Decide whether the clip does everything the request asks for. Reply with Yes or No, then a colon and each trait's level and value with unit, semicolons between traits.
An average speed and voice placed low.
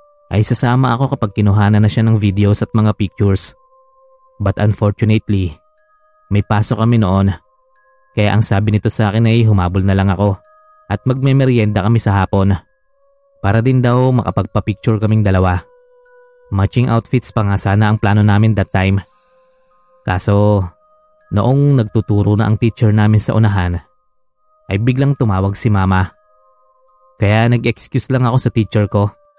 Yes: average, 145 wpm; low, 110 Hz